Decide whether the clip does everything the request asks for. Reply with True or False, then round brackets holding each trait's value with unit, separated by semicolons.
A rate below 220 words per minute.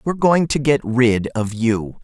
True (205 wpm)